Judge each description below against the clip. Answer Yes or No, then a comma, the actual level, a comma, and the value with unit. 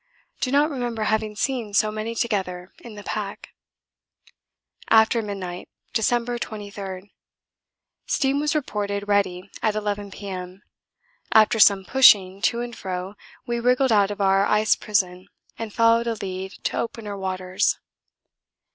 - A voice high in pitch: Yes, high, 210 Hz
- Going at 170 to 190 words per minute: No, slow, 135 wpm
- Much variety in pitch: No, average, 3.0 semitones